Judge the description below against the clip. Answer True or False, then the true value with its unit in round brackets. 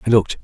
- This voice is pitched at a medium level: False (105 Hz)